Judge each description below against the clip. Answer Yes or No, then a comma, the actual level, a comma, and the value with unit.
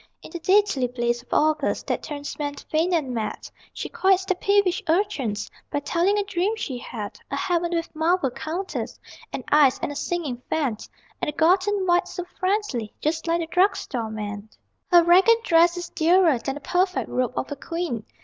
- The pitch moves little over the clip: No, wide, 5.4 semitones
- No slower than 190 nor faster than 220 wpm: Yes, average, 195 wpm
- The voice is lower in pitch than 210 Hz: No, very high, 330 Hz